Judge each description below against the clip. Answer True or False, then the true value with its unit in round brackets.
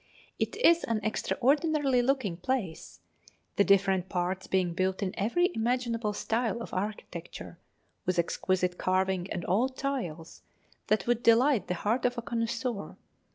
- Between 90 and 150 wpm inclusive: True (140 wpm)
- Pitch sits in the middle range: False (215 Hz)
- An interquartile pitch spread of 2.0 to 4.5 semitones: False (5.0 semitones)